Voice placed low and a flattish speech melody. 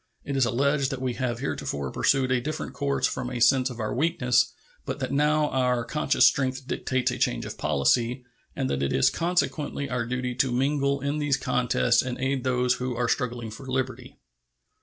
Yes: low, 130 Hz; narrow, 2.1 semitones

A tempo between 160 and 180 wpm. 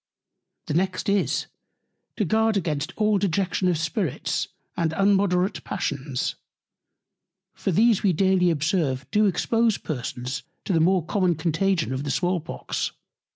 No: slow, 135 wpm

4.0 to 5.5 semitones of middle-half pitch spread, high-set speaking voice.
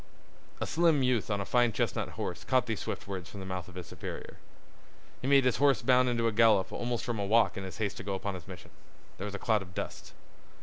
No: average, 4.3 semitones; low, 110 Hz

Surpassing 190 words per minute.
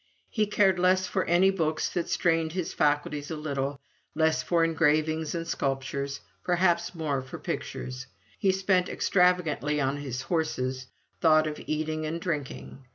No: average, 150 wpm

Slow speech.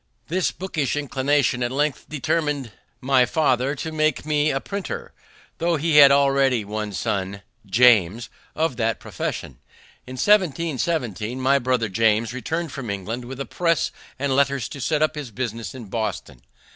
No: average, 155 wpm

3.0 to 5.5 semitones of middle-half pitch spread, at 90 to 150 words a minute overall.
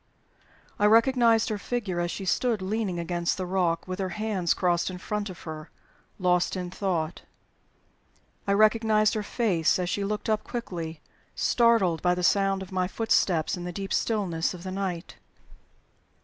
No: average, 3.3 semitones; average, 165 wpm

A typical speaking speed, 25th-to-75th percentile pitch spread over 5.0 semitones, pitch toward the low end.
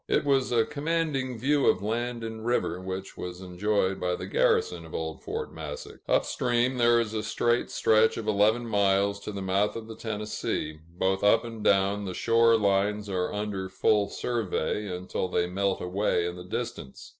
No: average, 185 wpm; average, 3.6 semitones; low, 105 Hz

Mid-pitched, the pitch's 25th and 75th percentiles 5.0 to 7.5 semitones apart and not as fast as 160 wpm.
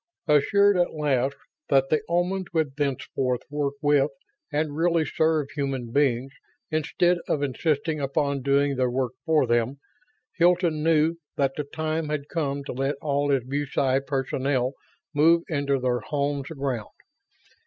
No: medium, 145 Hz; narrow, 2.5 semitones; average, 145 wpm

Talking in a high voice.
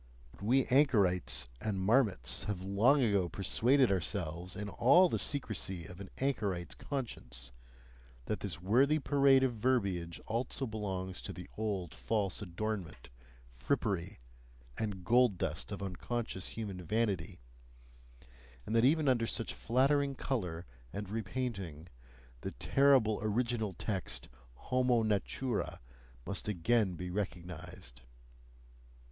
No: low, 105 Hz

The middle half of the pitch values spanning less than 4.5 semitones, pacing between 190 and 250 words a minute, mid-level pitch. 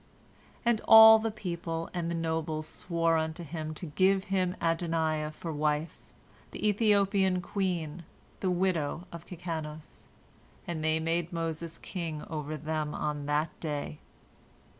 No: narrow, 2.6 semitones; slow, 135 wpm; medium, 165 Hz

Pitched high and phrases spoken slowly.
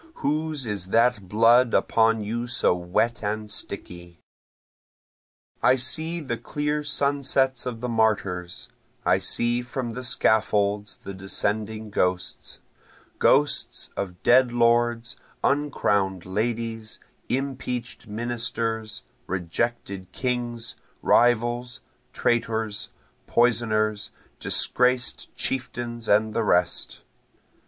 No: low, 115 Hz; slow, 95 wpm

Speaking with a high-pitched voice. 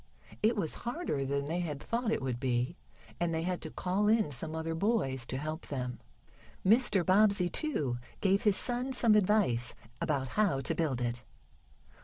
No: medium, 170 Hz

